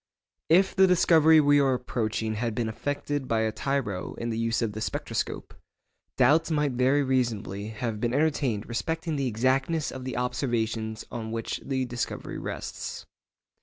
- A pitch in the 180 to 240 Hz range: No, low, 125 Hz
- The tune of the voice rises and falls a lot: No, average, 4.3 semitones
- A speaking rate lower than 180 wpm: Yes, average, 160 wpm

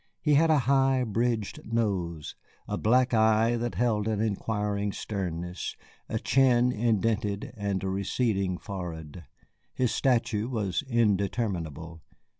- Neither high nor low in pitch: No, low, 110 Hz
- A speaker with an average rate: No, slow, 120 wpm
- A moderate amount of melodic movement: Yes, average, 3.8 semitones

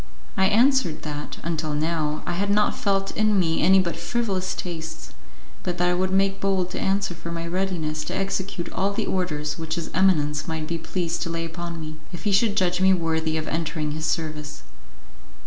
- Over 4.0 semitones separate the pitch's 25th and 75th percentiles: No, average, 3.2 semitones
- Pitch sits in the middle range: Yes, medium, 170 Hz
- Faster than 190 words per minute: Yes, average, 200 wpm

